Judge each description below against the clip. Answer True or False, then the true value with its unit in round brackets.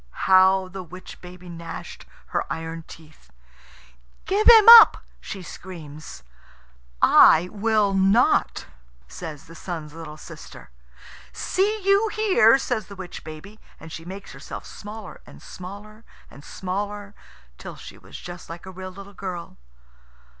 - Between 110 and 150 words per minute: True (135 wpm)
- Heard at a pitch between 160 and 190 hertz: True (185 Hz)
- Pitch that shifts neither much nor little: True (3.9 semitones)